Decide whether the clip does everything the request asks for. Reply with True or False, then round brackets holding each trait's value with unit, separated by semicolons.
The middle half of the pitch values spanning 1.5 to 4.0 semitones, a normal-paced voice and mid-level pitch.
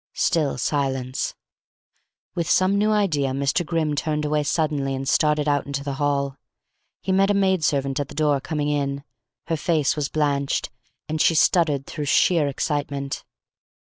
True (2.4 semitones; 160 wpm; 145 Hz)